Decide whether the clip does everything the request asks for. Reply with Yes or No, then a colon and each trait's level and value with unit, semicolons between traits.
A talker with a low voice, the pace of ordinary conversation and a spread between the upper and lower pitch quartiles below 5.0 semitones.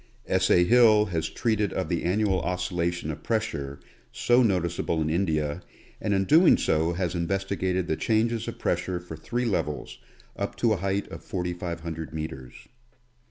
Yes: very low, 90 Hz; average, 160 wpm; average, 4.2 semitones